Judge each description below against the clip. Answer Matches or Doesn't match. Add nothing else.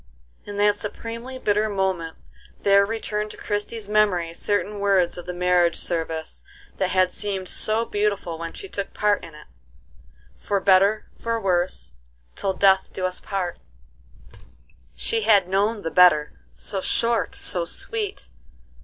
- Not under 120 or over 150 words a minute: Matches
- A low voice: Doesn't match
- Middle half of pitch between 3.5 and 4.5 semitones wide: Doesn't match